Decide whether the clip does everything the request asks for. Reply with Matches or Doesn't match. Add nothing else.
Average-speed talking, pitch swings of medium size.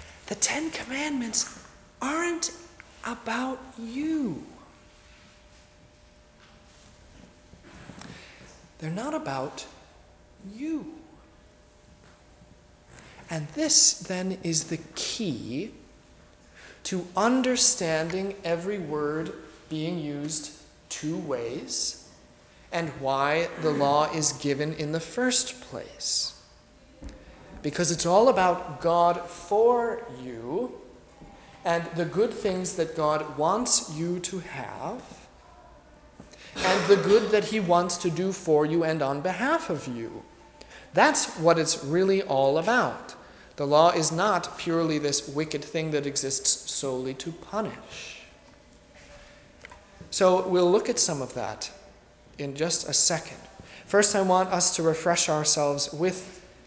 Doesn't match